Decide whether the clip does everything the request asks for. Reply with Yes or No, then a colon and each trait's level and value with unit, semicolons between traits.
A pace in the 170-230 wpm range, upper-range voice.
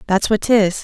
Yes: fast, 215 wpm; high, 205 Hz